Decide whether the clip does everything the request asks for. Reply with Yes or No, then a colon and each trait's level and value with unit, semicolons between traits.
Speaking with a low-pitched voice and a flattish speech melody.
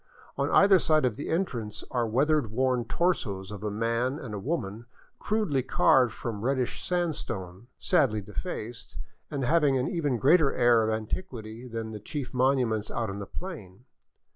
No: low, 125 Hz; average, 5.0 semitones